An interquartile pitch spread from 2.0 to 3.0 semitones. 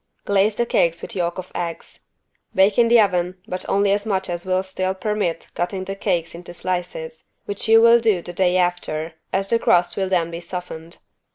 Yes: narrow, 2.4 semitones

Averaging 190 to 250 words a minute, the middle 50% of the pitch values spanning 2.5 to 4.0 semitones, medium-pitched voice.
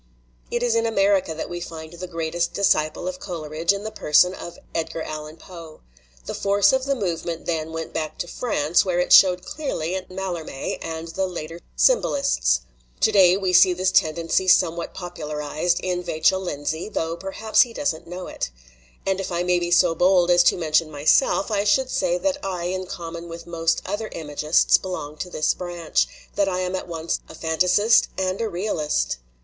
Yes: average, 195 wpm; average, 2.8 semitones; medium, 175 Hz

